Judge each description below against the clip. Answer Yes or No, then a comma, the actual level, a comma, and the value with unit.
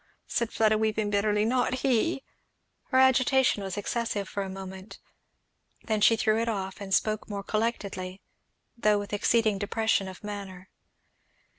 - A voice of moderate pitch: No, high, 215 Hz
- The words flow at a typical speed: Yes, average, 150 wpm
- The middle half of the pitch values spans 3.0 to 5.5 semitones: No, narrow, 2.5 semitones